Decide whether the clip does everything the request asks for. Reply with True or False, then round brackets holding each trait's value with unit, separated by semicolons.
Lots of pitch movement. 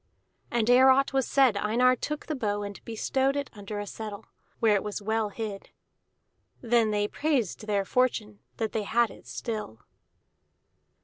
False (3.5 semitones)